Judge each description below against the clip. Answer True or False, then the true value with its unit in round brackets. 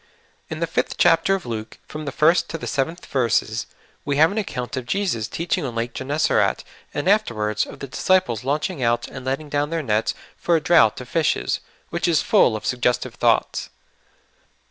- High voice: False (140 Hz)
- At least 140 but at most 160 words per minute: False (190 wpm)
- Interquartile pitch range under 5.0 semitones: False (5.6 semitones)